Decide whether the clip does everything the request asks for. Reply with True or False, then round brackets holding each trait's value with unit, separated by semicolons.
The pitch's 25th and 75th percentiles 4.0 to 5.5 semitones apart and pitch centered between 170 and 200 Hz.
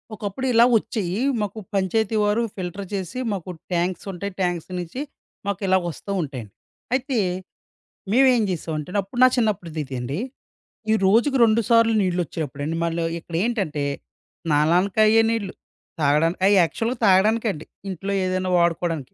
True (4.9 semitones; 190 Hz)